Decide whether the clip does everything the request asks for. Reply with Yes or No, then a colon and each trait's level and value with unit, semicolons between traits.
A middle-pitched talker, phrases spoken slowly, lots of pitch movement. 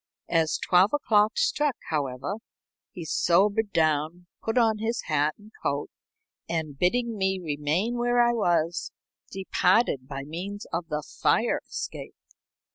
Yes: medium, 180 Hz; slow, 130 wpm; wide, 6.1 semitones